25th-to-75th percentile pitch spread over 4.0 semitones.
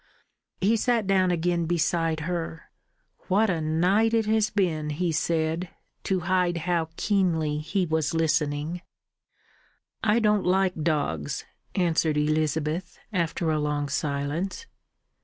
No: average, 3.1 semitones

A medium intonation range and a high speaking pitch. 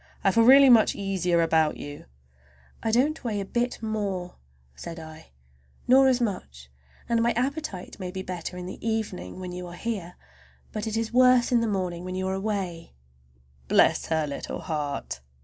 Yes: average, 5.0 semitones; high, 195 Hz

